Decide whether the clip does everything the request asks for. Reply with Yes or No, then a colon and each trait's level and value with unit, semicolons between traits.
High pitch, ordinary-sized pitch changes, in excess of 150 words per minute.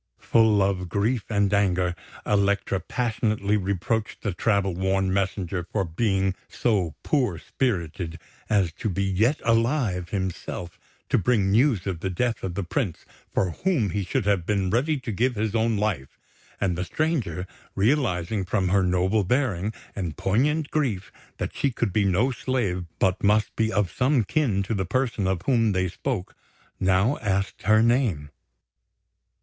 No: low, 100 Hz; average, 3.7 semitones; average, 160 wpm